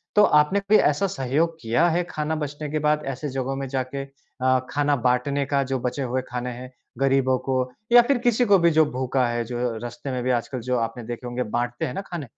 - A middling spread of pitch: Yes, average, 3.2 semitones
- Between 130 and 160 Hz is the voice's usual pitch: Yes, low, 135 Hz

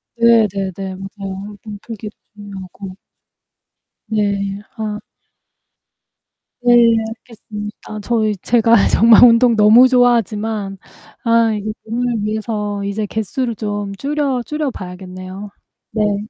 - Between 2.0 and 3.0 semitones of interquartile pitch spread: Yes, narrow, 2.5 semitones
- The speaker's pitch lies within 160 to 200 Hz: No, high, 215 Hz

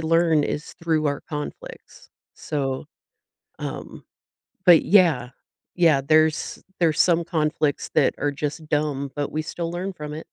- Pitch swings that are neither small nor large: No, narrow, 2.3 semitones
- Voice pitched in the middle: Yes, medium, 155 Hz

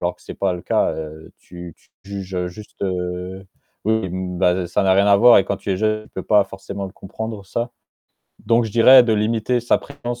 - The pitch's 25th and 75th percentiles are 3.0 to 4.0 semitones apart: Yes, average, 3.4 semitones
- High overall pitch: No, low, 100 Hz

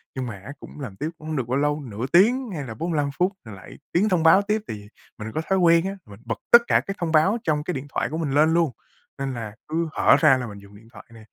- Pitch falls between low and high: Yes, medium, 150 Hz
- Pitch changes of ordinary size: No, wide, 6.3 semitones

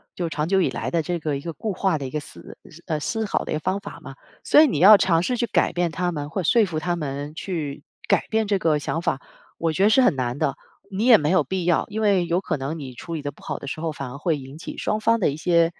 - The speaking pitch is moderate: Yes, medium, 170 Hz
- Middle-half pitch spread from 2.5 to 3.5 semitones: No, average, 4.3 semitones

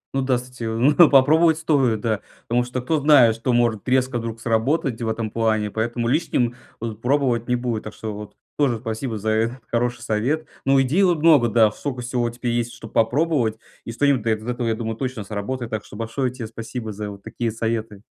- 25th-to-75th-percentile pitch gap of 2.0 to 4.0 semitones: Yes, average, 2.8 semitones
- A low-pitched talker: Yes, low, 120 Hz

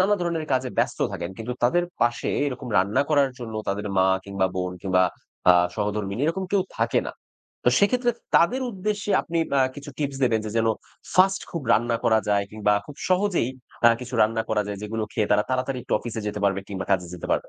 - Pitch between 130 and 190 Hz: No, low, 120 Hz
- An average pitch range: No, wide, 8.0 semitones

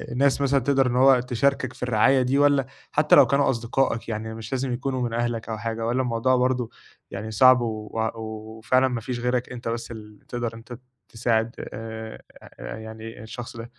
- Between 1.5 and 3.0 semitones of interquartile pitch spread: Yes, narrow, 2.4 semitones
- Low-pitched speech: Yes, low, 120 Hz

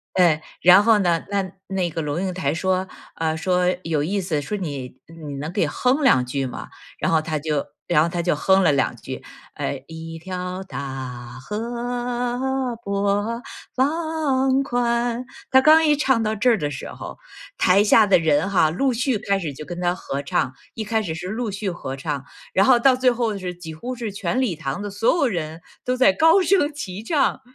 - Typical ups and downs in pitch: No, wide, 6.9 semitones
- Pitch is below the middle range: No, high, 190 Hz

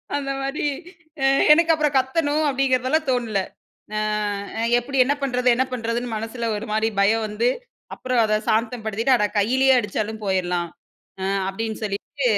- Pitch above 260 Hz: No, high, 235 Hz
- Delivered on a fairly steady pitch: No, average, 3.7 semitones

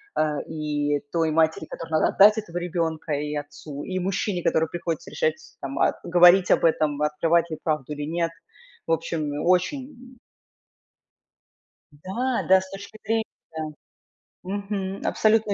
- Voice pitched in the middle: Yes, medium, 170 Hz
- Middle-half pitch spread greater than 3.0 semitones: Yes, average, 4.1 semitones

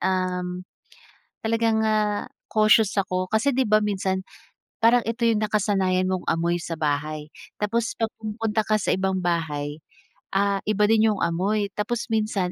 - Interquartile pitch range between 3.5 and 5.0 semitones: No, average, 3.1 semitones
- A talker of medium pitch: No, high, 205 Hz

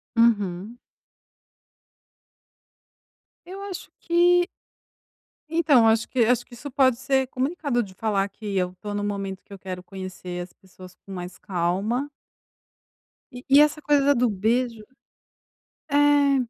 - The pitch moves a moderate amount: No, wide, 6.4 semitones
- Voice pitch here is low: No, high, 230 Hz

